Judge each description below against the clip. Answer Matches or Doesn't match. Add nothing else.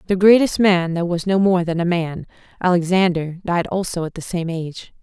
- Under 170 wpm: Doesn't match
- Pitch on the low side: Doesn't match